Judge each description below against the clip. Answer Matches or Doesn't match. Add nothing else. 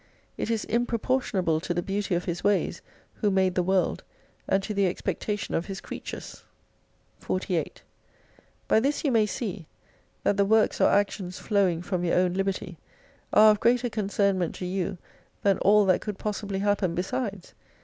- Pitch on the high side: Matches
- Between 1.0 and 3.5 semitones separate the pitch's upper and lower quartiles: Matches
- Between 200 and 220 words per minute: Doesn't match